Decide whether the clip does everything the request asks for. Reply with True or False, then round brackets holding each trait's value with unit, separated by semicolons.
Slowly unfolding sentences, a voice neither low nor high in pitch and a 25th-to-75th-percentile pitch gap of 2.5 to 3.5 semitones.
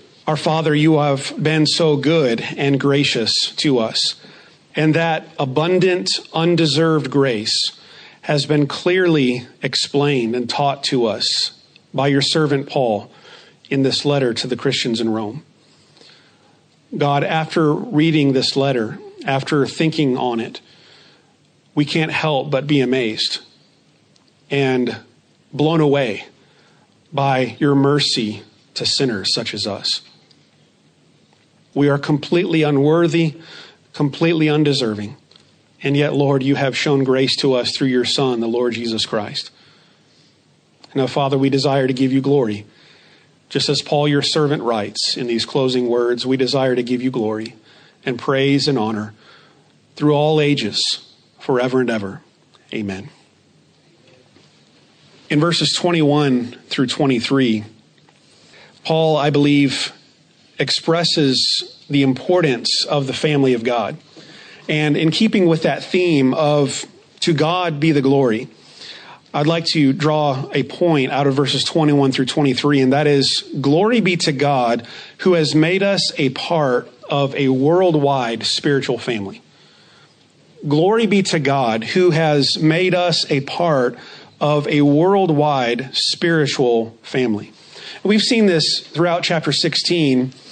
True (130 wpm; 145 Hz; 3.2 semitones)